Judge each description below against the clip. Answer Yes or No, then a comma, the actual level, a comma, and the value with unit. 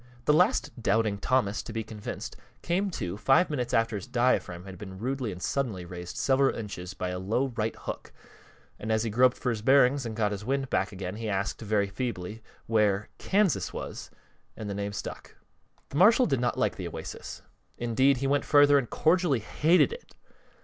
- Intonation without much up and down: No, average, 5.1 semitones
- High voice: No, low, 115 Hz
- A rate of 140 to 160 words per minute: No, average, 190 wpm